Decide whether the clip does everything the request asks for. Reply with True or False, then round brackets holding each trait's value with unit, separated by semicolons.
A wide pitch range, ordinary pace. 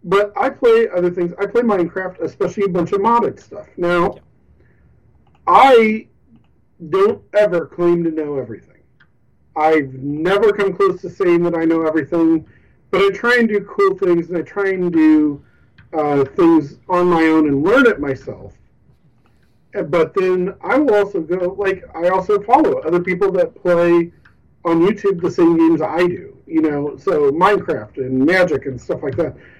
False (3.5 semitones; 170 wpm)